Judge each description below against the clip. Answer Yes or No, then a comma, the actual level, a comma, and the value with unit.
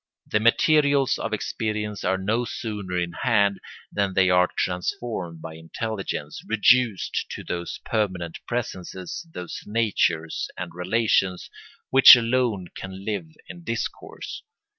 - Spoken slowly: Yes, slow, 120 wpm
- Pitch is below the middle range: Yes, low, 100 Hz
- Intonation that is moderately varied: Yes, average, 4.2 semitones